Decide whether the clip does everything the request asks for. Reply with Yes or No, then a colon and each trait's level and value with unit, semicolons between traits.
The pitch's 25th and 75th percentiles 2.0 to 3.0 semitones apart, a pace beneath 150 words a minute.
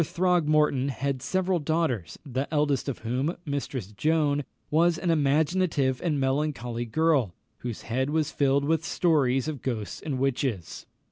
No: average, 3.5 semitones; average, 140 wpm